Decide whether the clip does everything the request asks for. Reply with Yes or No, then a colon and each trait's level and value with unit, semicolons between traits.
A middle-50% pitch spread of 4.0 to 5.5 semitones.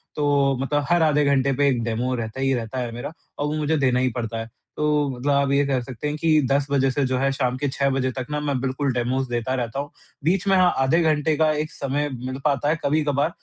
No: narrow, 2.4 semitones